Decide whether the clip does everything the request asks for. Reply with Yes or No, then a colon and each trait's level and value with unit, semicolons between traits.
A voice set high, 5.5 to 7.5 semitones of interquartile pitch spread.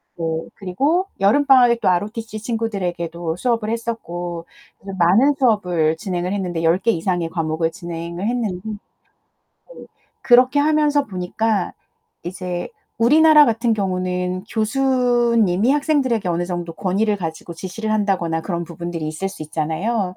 No: high, 195 Hz; average, 5.1 semitones